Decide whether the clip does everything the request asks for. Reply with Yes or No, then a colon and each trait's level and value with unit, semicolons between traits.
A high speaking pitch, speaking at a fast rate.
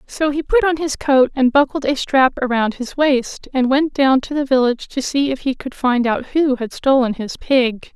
Yes: very high, 265 Hz; fast, 235 wpm